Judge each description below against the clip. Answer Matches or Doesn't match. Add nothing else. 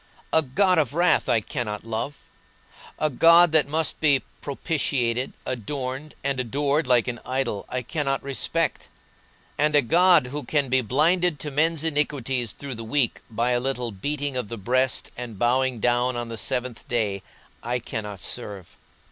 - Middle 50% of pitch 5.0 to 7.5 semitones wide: Doesn't match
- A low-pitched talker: Matches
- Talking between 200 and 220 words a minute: Doesn't match